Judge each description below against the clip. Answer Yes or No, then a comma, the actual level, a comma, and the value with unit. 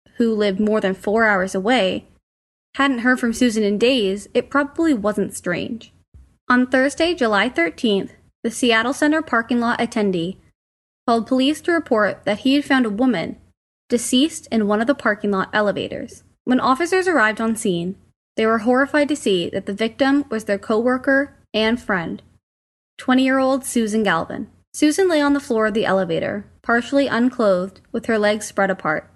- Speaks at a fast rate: No, average, 170 wpm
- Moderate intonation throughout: Yes, average, 4.3 semitones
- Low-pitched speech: No, high, 230 Hz